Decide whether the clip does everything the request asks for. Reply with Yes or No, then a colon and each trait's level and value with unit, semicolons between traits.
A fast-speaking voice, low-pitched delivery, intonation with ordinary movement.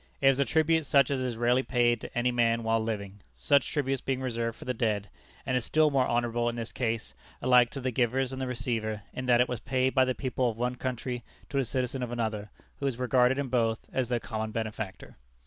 No: fast, 235 wpm; low, 125 Hz; narrow, 2.2 semitones